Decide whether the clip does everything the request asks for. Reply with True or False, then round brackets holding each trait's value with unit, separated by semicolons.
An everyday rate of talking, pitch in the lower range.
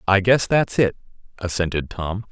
True (155 wpm; 100 Hz)